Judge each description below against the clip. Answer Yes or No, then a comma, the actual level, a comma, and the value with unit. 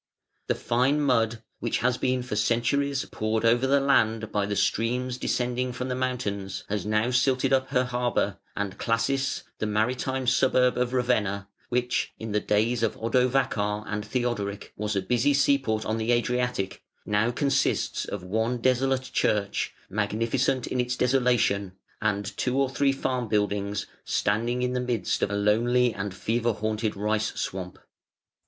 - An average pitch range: Yes, average, 3.3 semitones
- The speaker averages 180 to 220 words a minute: No, average, 160 wpm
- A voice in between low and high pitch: No, low, 120 Hz